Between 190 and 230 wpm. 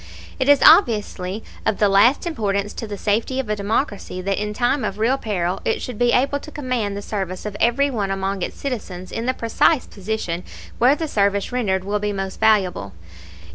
Yes: average, 200 wpm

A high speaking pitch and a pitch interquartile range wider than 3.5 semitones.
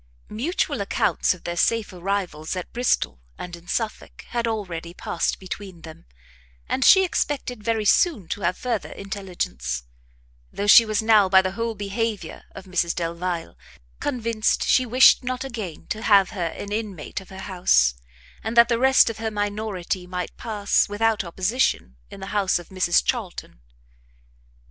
Yes: high, 200 Hz; average, 4.1 semitones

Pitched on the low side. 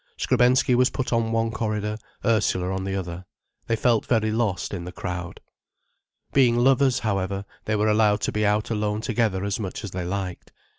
Yes: low, 105 Hz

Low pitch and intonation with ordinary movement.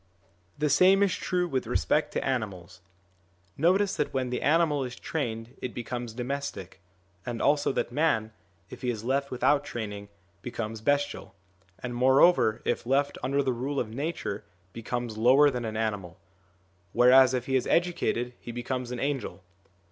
Yes: low, 125 Hz; average, 3.7 semitones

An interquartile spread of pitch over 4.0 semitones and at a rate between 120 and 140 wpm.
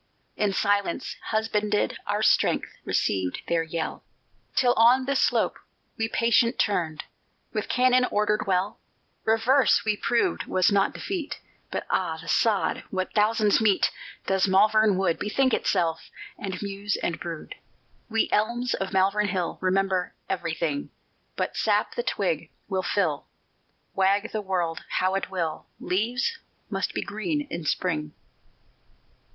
No: average, 3.4 semitones; slow, 135 wpm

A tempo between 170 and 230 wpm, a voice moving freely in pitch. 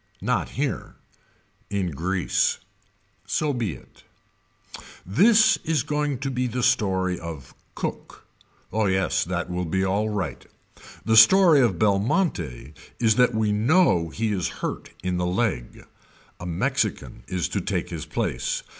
No: slow, 135 wpm; wide, 5.8 semitones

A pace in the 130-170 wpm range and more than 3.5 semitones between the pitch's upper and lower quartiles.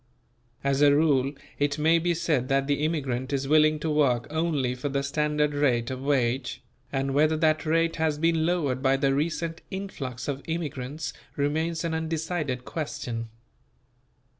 No: average, 160 wpm; average, 2.9 semitones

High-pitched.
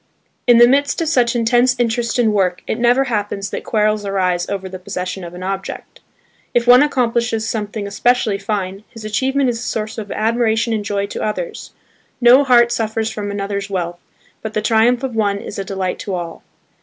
Yes: high, 220 Hz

